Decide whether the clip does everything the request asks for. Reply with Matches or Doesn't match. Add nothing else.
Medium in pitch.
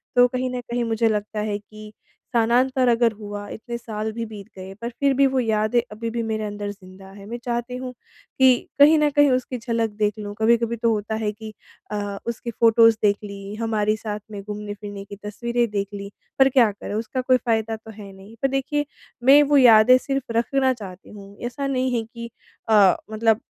Doesn't match